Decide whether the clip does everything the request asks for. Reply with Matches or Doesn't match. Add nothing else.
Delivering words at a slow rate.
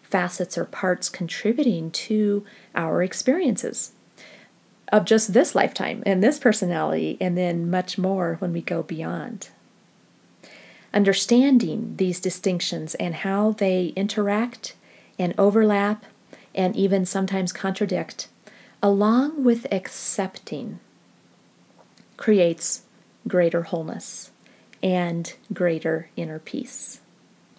Matches